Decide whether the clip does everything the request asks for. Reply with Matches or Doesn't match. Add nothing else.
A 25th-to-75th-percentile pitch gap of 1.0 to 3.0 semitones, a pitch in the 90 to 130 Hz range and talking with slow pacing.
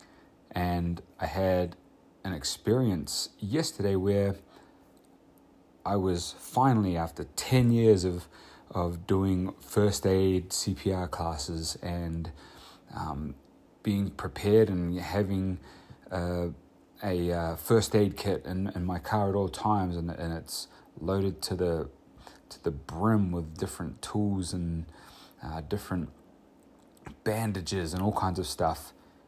Matches